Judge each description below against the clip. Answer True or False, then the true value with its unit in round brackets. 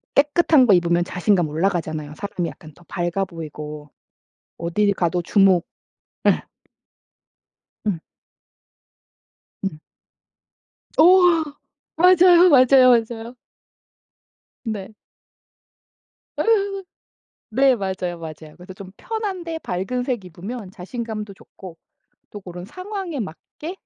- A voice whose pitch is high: True (200 Hz)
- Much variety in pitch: True (8.0 semitones)